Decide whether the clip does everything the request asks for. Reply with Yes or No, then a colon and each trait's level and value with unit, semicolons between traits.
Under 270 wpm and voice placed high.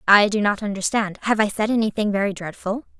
Yes: average, 200 wpm; high, 210 Hz